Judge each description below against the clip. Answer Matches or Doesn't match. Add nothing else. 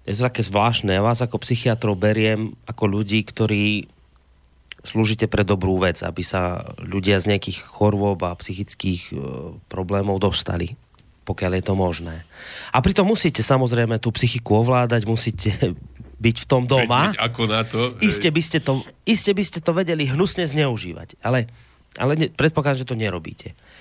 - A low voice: Matches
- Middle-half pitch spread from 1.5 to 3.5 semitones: Doesn't match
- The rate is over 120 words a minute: Matches